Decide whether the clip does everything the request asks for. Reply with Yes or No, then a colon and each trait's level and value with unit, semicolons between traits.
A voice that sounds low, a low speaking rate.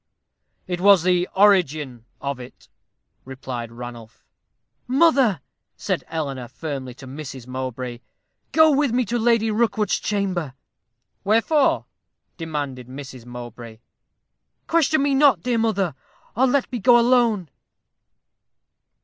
No: medium, 175 Hz; slow, 115 wpm